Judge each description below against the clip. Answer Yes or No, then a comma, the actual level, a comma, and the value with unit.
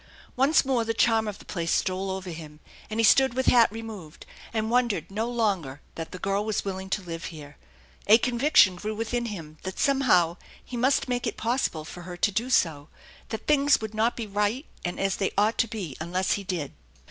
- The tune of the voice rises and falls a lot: No, average, 4.6 semitones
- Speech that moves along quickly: Yes, fast, 210 wpm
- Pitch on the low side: No, high, 210 Hz